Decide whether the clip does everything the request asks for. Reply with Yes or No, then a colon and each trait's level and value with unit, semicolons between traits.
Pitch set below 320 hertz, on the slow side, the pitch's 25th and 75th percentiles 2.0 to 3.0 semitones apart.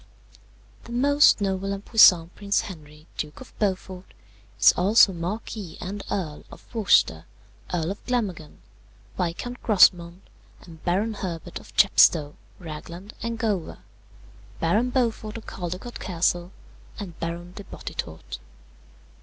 No: medium, 185 Hz; slow, 120 wpm; average, 4.1 semitones